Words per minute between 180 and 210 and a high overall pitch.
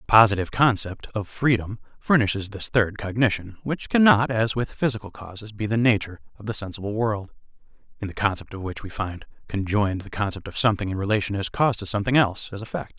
No: average, 200 wpm; low, 105 Hz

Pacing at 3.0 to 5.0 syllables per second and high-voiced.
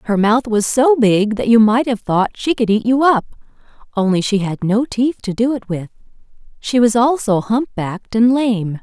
Yes: 4.8 syllables/s; high, 225 Hz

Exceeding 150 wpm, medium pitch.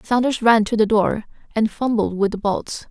No: fast, 205 wpm; high, 220 Hz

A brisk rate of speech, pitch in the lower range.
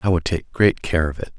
Yes: fast, 305 wpm; very low, 85 Hz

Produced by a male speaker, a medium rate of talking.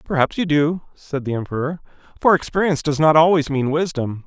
Yes: male; average, 185 wpm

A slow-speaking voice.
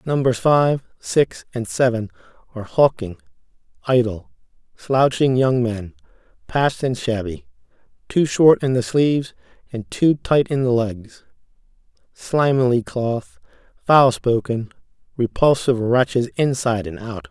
Yes: slow, 120 wpm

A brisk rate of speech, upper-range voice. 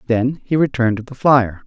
No: fast, 215 wpm; low, 125 Hz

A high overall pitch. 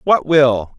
No: medium, 140 Hz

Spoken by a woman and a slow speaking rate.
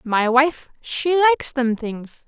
Yes: female; slow, 130 wpm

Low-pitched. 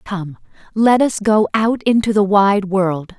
No: high, 205 Hz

